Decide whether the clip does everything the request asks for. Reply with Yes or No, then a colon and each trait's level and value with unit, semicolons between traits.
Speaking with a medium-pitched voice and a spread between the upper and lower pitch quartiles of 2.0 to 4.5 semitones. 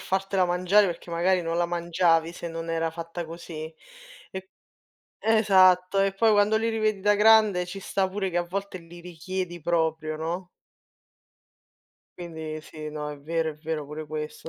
Yes: medium, 175 Hz; average, 2.8 semitones